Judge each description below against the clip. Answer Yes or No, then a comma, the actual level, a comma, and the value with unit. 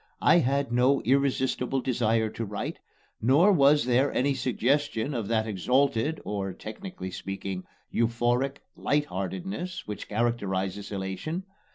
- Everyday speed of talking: No, slow, 125 wpm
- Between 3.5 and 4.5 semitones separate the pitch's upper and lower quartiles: No, average, 5.0 semitones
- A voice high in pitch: No, low, 120 Hz